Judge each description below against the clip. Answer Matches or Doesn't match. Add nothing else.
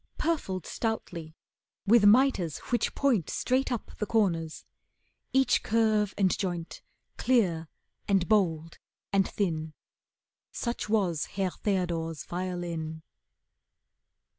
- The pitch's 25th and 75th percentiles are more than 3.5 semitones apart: Matches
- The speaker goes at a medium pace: Doesn't match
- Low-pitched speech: Doesn't match